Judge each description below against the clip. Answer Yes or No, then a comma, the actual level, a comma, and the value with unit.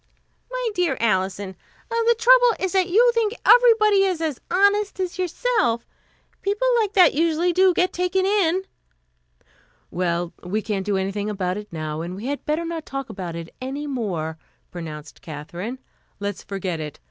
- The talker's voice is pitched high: Yes, very high, 290 Hz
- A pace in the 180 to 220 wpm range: No, average, 160 wpm